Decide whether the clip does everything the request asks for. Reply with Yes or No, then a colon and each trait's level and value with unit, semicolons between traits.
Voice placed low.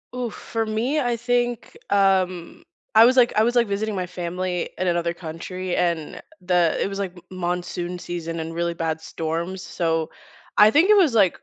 No: medium, 185 Hz